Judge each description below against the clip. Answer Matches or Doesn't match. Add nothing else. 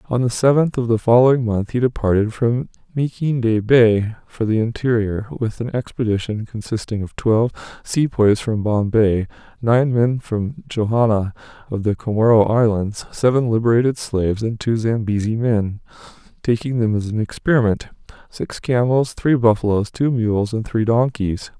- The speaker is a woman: Doesn't match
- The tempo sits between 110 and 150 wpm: Matches